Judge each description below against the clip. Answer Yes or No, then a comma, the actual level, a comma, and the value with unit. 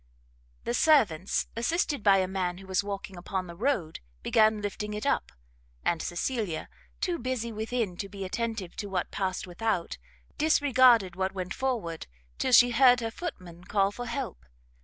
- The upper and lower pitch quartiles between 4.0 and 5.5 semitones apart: Yes, average, 4.7 semitones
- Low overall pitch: No, high, 210 Hz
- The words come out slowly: No, average, 160 wpm